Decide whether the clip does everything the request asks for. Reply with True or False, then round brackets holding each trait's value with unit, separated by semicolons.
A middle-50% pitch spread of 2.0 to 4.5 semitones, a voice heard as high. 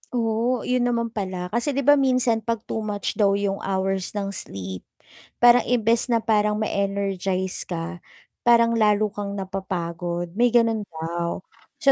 True (3.6 semitones; 210 Hz)